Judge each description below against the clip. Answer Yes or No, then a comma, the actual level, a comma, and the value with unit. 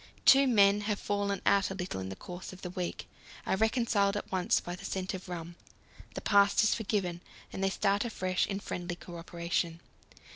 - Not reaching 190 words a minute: No, fast, 205 wpm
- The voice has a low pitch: No, high, 190 Hz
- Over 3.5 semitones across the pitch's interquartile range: No, narrow, 2.4 semitones